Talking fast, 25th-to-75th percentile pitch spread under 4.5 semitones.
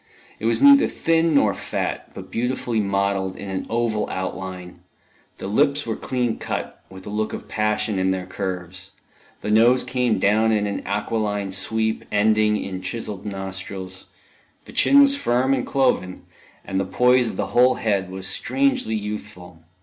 No: average, 165 wpm; average, 4.1 semitones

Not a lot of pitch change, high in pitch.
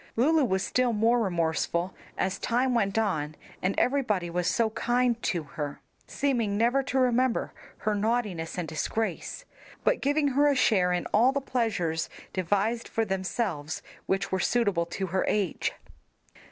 No: average, 5.3 semitones; high, 215 Hz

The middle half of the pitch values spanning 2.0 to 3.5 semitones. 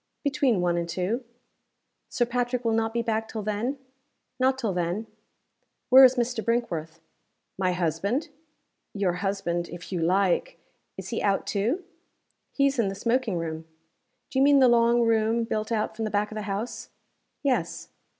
No: average, 4.3 semitones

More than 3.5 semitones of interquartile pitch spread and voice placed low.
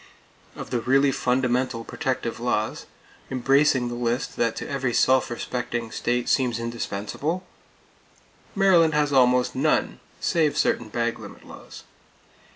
No: narrow, 2.5 semitones; low, 125 Hz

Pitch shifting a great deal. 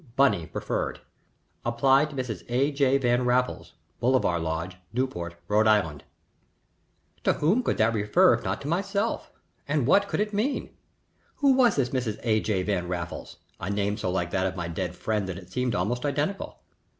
Yes: wide, 6.8 semitones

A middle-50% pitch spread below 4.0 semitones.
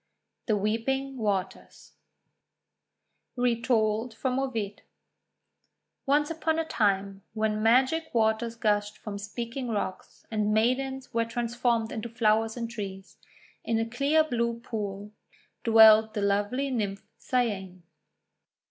Yes: average, 2.9 semitones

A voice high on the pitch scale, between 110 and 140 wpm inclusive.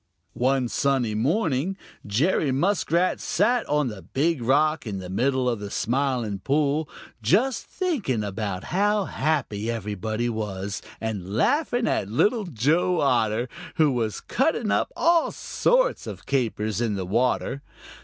No: low, 130 Hz; slow, 135 wpm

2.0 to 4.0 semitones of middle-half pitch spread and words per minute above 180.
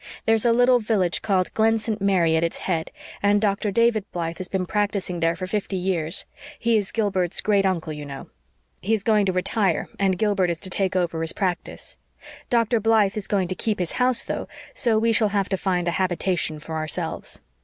Yes: average, 3.5 semitones; fast, 205 wpm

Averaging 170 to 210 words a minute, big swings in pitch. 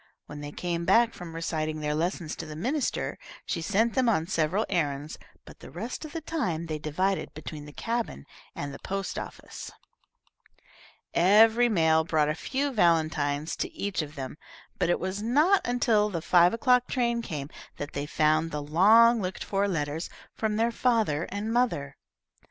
Yes: average, 175 wpm; wide, 6.6 semitones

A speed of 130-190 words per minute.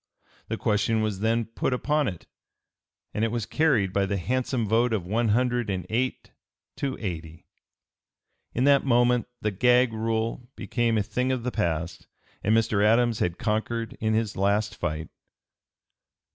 Yes: average, 160 wpm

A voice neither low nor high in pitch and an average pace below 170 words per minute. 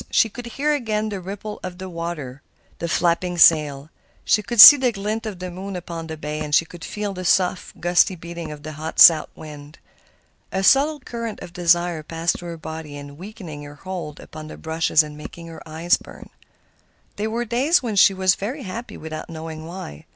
No: medium, 175 Hz; average, 195 wpm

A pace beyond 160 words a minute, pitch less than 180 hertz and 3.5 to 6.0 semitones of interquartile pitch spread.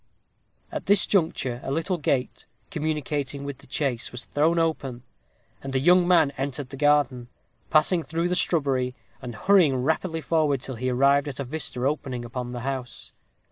Yes: average, 170 wpm; medium, 140 Hz; average, 3.8 semitones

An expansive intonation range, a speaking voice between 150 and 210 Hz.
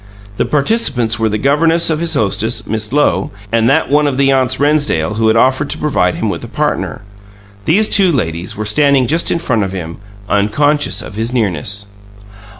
No: wide, 5.9 semitones; low, 125 Hz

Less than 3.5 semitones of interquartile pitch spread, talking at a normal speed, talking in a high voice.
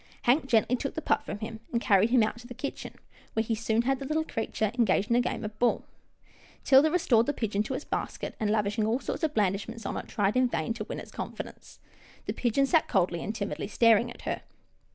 No: average, 3.1 semitones; fast, 235 wpm; high, 230 Hz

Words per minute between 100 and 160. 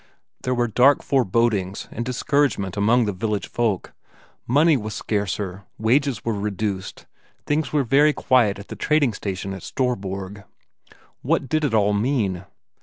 Yes: average, 145 wpm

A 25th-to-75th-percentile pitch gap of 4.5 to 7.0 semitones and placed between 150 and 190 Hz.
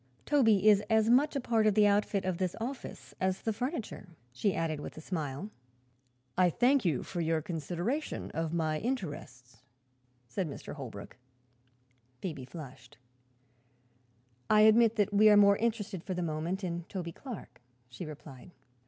Yes: wide, 5.4 semitones; medium, 185 Hz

